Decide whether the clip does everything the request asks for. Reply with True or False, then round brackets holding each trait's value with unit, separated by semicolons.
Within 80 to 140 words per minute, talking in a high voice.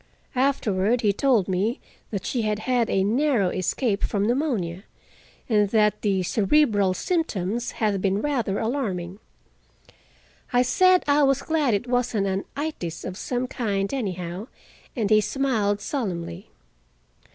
True (135 wpm; 215 Hz)